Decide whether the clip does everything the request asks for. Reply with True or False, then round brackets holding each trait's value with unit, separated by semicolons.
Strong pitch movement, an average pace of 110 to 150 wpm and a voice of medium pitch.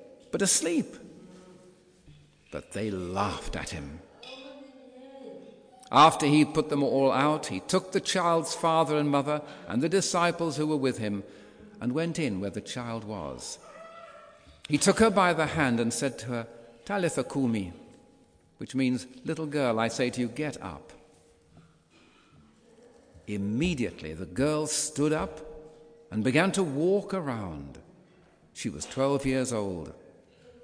True (7.8 semitones; 140 wpm; 150 Hz)